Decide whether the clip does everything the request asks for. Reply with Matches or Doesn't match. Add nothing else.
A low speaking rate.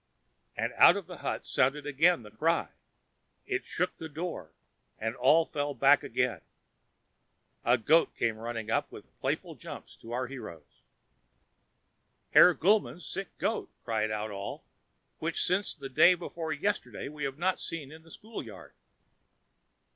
Doesn't match